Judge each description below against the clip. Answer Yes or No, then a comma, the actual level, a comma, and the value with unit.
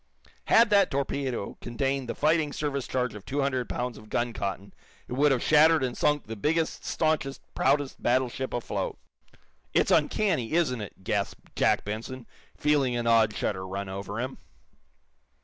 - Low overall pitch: Yes, low, 130 Hz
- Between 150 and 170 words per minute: Yes, average, 160 wpm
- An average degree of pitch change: Yes, average, 4.4 semitones